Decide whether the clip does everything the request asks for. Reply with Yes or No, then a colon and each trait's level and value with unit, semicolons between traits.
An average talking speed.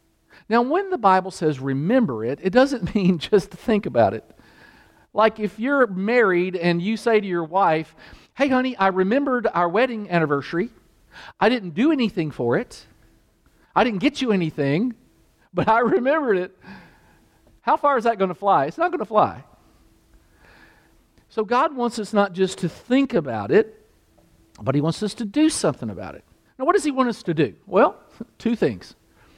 Yes: average, 180 wpm